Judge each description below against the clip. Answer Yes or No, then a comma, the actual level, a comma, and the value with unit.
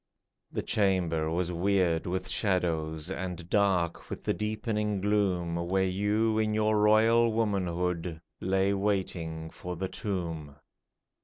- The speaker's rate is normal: No, slow, 125 wpm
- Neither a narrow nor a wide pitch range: Yes, average, 3.5 semitones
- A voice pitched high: No, very low, 95 Hz